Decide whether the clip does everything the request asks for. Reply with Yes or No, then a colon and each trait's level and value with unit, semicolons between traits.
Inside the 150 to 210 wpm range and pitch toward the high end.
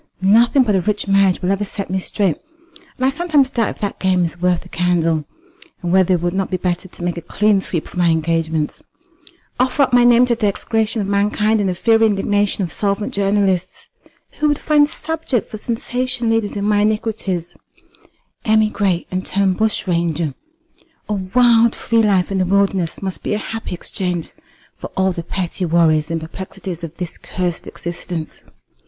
Yes: average, 185 wpm; high, 195 Hz